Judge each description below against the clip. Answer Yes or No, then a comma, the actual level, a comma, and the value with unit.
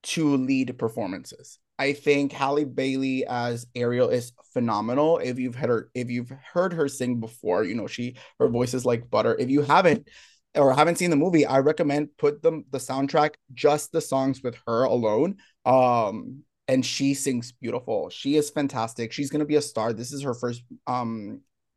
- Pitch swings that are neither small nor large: Yes, average, 3.1 semitones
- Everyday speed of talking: Yes, average, 185 wpm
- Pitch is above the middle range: No, low, 135 Hz